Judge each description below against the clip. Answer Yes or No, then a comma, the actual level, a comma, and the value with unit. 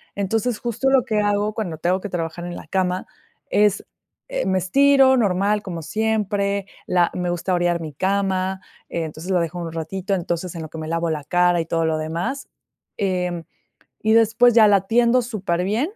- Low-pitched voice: No, high, 190 Hz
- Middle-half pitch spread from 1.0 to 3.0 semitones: No, average, 3.8 semitones